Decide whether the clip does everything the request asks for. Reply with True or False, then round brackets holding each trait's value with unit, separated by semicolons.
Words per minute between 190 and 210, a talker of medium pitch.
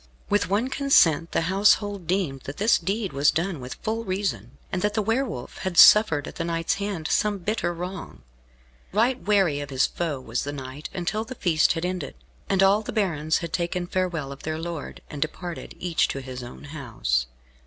True (195 wpm; 175 Hz)